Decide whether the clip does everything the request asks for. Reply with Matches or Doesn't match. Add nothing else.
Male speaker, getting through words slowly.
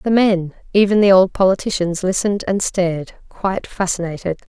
Doesn't match